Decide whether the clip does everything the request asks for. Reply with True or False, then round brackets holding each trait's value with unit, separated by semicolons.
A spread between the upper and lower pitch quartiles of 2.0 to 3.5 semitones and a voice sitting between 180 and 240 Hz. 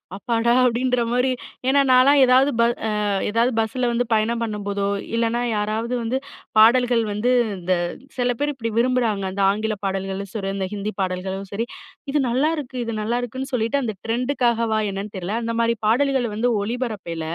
True (3.2 semitones; 230 Hz)